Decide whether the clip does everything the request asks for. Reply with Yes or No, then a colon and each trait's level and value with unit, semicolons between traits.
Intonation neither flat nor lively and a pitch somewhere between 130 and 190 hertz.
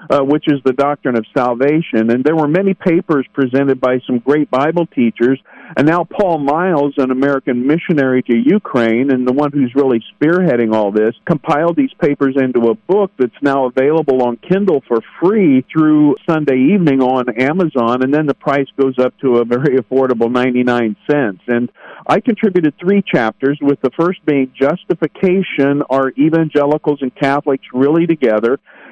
Yes: average, 3.5 semitones; medium, 140 Hz